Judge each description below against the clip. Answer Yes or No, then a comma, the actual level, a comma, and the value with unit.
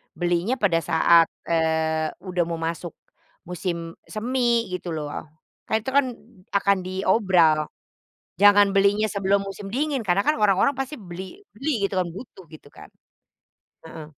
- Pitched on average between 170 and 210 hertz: Yes, high, 190 Hz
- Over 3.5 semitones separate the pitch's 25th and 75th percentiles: Yes, average, 4.2 semitones